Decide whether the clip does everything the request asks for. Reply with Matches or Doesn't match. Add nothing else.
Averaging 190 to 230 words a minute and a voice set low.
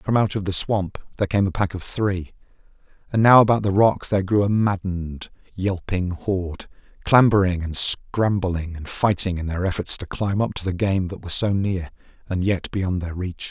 Matches